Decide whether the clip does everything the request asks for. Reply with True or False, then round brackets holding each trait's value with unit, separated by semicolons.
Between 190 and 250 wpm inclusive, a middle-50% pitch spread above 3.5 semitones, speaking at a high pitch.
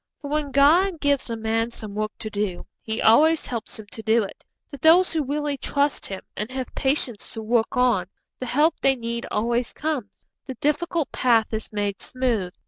True (195 wpm; 4.6 semitones; 245 Hz)